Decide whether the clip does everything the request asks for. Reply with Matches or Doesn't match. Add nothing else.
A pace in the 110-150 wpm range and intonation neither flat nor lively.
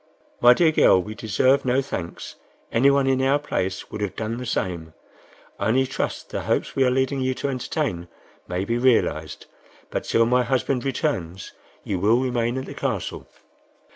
Doesn't match